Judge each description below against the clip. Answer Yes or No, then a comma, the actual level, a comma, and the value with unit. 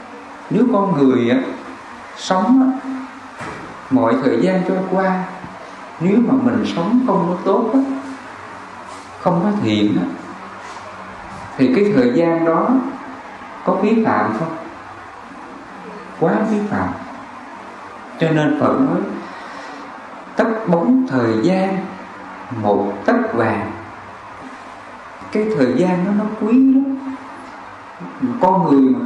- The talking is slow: Yes, slow, 115 wpm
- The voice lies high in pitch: Yes, high, 205 Hz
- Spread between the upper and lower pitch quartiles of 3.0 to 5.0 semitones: No, wide, 5.5 semitones